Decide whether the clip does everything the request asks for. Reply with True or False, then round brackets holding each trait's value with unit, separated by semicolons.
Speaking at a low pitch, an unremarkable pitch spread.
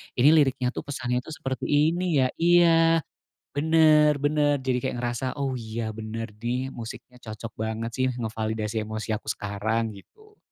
True (125 Hz; 4.9 semitones)